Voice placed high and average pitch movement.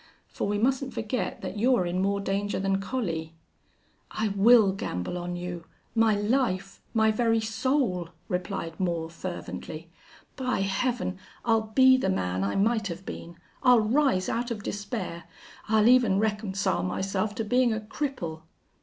Yes: high, 205 Hz; average, 4.2 semitones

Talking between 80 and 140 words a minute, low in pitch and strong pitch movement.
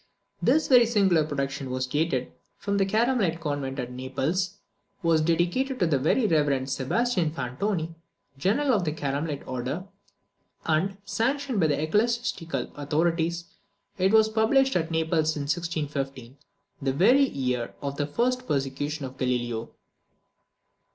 No: slow, 135 wpm; medium, 160 Hz; wide, 6.5 semitones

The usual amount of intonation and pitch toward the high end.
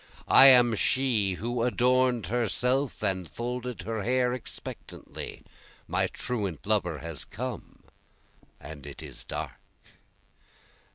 No: average, 4.4 semitones; low, 120 Hz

